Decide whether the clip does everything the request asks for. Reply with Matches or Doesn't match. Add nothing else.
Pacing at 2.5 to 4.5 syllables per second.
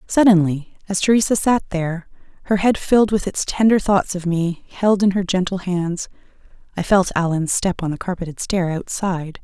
Doesn't match